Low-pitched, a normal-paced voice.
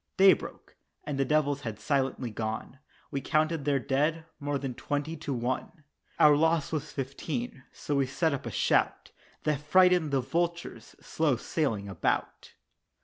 No: medium, 145 Hz; average, 155 wpm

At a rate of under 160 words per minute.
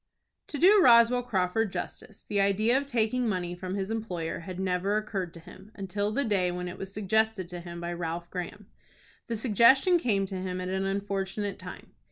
No: average, 195 wpm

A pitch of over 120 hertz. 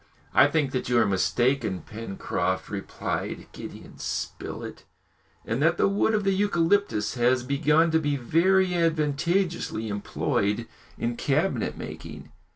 Yes: medium, 140 Hz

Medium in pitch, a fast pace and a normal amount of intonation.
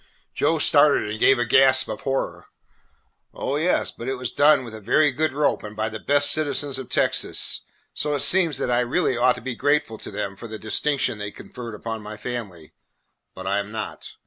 No: low, 125 Hz; fast, 215 wpm; average, 4.7 semitones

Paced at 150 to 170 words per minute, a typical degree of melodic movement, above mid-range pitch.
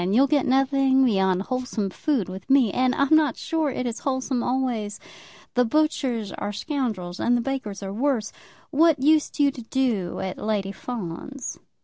Yes: average, 165 wpm; average, 4.7 semitones; very high, 250 Hz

